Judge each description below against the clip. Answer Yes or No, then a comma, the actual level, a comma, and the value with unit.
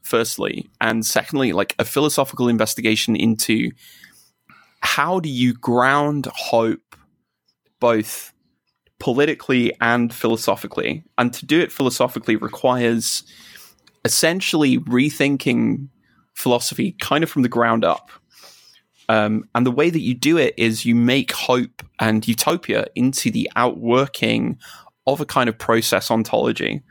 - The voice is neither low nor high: No, low, 125 Hz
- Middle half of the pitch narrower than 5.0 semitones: Yes, average, 3.7 semitones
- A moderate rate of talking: No, slow, 125 wpm